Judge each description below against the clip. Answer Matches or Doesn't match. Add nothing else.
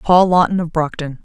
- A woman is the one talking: Matches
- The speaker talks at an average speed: Matches